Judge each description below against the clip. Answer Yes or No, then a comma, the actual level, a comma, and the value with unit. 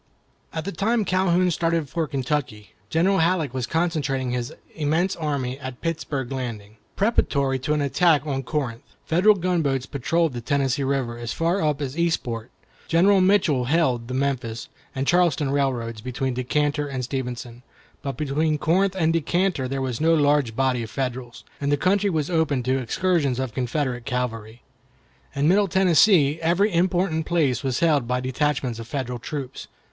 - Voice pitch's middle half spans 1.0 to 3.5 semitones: No, average, 4.6 semitones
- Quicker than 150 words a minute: Yes, average, 160 wpm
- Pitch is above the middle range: No, medium, 140 Hz